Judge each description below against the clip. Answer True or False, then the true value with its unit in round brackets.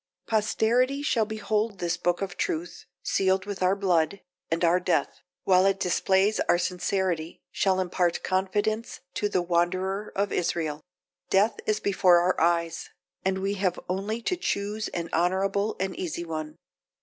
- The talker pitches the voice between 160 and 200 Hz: True (190 Hz)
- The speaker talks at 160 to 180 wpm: False (150 wpm)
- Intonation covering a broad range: False (2.7 semitones)